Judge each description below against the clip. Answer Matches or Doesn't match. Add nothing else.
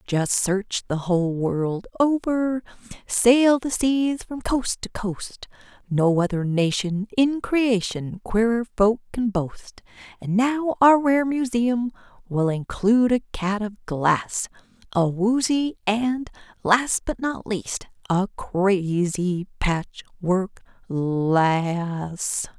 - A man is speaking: Doesn't match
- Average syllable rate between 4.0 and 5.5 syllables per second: Doesn't match